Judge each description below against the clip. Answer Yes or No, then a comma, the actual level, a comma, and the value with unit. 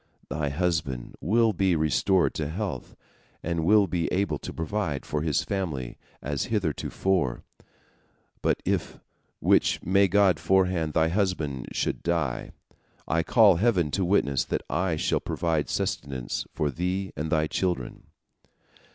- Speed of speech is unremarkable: No, slow, 130 wpm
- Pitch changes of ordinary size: Yes, average, 4.2 semitones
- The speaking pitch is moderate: No, very low, 85 Hz